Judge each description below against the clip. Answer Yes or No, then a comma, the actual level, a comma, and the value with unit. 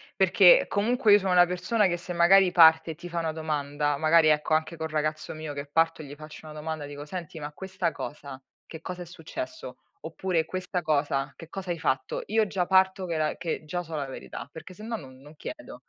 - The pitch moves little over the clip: No, average, 3.3 semitones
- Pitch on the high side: No, medium, 165 Hz